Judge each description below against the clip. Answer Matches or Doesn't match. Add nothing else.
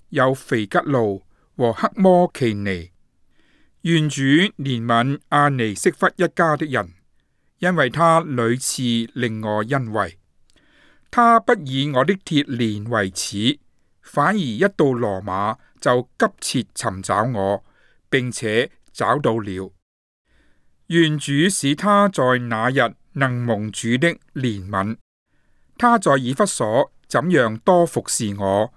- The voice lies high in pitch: Doesn't match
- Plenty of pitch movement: Matches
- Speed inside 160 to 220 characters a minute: Matches